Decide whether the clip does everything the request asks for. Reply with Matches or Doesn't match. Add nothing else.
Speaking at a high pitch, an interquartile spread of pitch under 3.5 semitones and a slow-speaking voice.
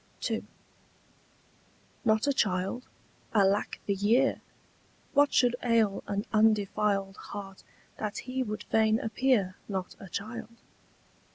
Matches